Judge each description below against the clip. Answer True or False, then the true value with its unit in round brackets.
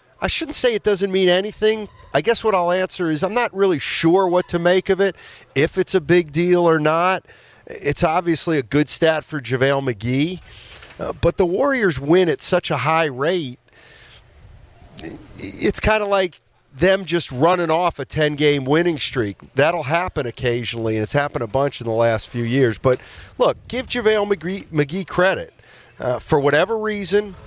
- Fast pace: False (180 wpm)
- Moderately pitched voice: True (170 Hz)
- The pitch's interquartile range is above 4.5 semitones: True (5.1 semitones)